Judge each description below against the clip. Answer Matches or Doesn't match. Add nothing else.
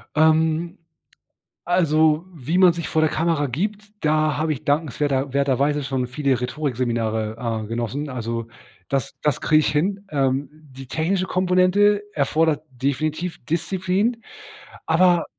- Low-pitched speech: Doesn't match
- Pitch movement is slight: Doesn't match